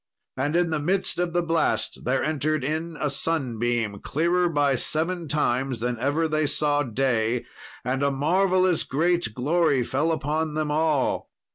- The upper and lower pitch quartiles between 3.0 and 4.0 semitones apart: Yes, average, 3.7 semitones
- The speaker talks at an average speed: Yes, average, 155 wpm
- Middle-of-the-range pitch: Yes, medium, 150 Hz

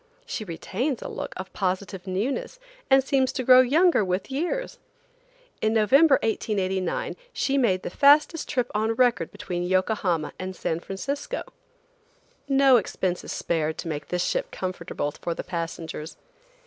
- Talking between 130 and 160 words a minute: Yes, average, 150 wpm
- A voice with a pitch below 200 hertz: No, high, 210 Hz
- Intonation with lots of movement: Yes, wide, 6.8 semitones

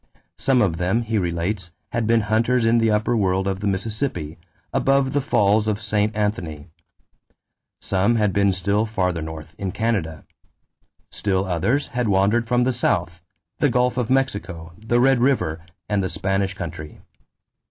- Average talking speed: Yes, average, 160 wpm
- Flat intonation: No, average, 4.2 semitones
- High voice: No, low, 105 Hz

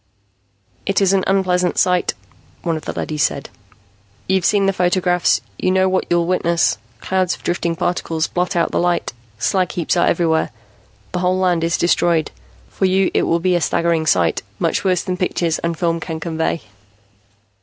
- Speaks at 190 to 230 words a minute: No, average, 175 wpm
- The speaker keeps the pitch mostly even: Yes, narrow, 1.8 semitones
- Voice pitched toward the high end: No, medium, 175 Hz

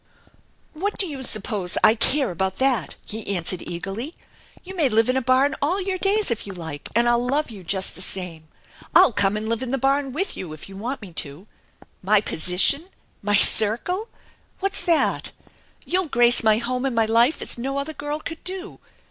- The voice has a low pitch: No, high, 240 Hz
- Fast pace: Yes, fast, 210 wpm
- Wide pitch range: Yes, wide, 6.6 semitones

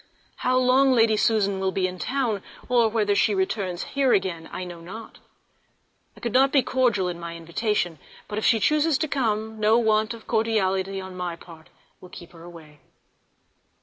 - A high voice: Yes, high, 210 Hz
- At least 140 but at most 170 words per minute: No, average, 180 wpm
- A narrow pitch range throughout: No, average, 4.3 semitones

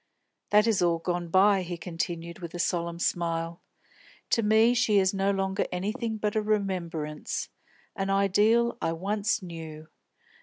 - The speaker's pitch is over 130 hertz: Yes, high, 190 Hz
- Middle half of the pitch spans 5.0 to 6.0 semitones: No, average, 3.6 semitones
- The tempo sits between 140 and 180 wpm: Yes, average, 150 wpm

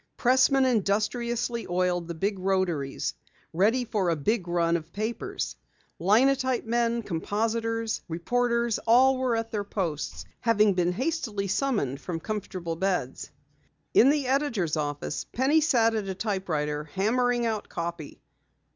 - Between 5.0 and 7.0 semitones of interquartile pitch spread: Yes, wide, 5.5 semitones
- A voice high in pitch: Yes, high, 210 Hz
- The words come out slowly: Yes, slow, 130 wpm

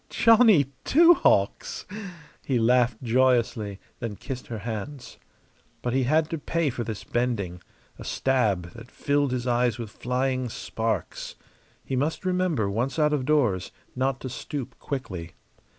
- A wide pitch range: No, average, 4.0 semitones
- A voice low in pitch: Yes, low, 125 Hz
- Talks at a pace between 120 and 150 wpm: Yes, average, 145 wpm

